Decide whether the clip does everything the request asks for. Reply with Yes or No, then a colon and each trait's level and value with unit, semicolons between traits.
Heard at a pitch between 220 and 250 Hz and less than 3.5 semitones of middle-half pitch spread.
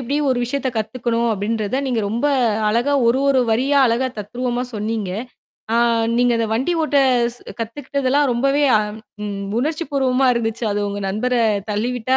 Yes: high, 240 Hz; average, 3.0 semitones